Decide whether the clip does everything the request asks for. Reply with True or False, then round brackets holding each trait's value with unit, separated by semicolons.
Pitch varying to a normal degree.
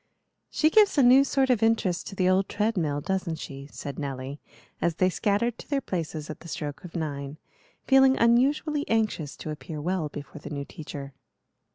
False (7.9 semitones)